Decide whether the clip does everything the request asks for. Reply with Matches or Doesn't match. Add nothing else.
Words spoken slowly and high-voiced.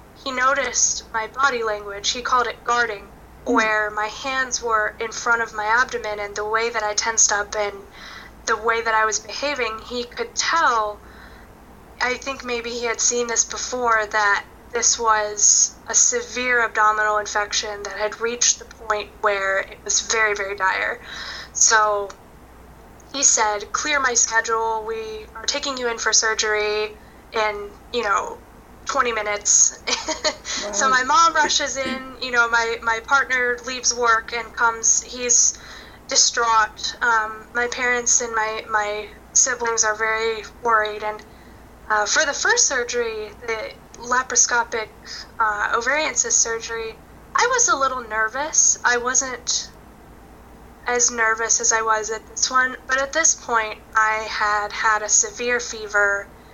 Doesn't match